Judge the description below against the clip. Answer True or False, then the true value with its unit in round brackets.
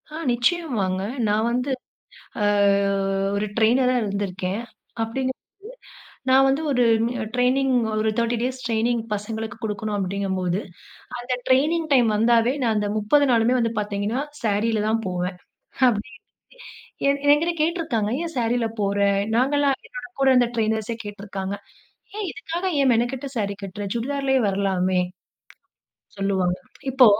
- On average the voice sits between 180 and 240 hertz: True (230 Hz)